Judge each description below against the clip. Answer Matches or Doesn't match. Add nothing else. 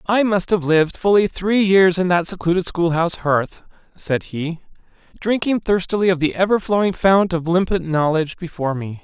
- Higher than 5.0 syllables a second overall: Matches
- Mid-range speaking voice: Matches